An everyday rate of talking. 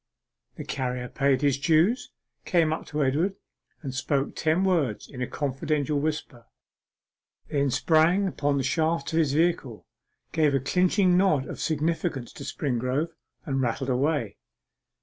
Yes: average, 145 wpm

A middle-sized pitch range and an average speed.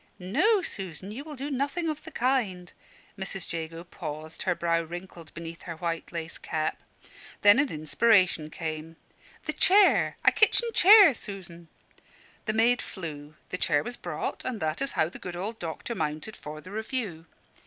No: wide, 6.9 semitones; average, 165 wpm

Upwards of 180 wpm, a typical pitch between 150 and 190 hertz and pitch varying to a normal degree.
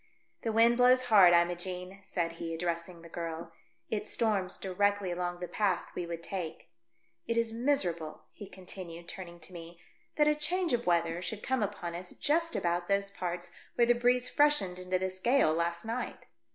Yes: average, 190 wpm; medium, 185 Hz; average, 5.0 semitones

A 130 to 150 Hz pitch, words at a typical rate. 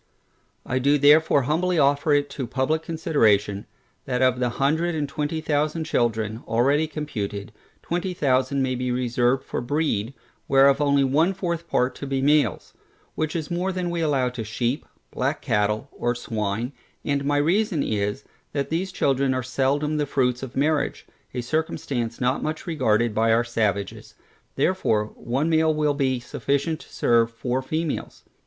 Yes: medium, 140 Hz; average, 160 wpm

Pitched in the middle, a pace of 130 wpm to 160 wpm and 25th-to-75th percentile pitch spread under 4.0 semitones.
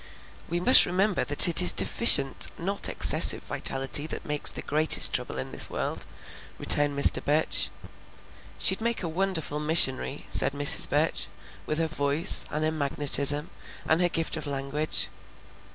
Yes: medium, 155 Hz; average, 150 wpm; average, 3.2 semitones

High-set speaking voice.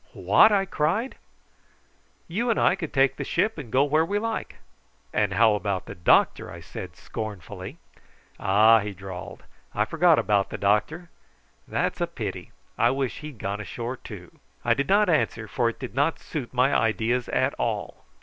No: low, 125 Hz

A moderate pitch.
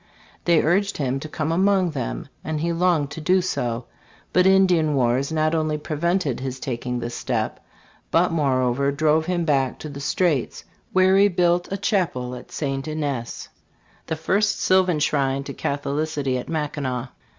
Yes: medium, 155 Hz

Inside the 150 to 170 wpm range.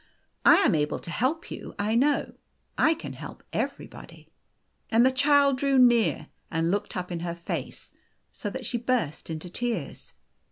Yes: average, 165 wpm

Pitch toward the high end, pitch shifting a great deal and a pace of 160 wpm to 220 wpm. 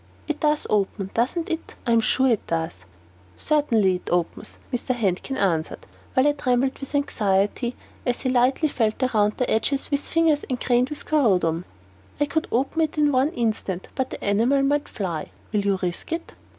Yes: high, 245 Hz; wide, 5.9 semitones; average, 180 wpm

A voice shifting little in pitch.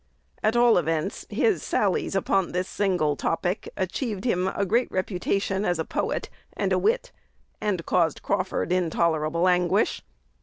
No: average, 3.4 semitones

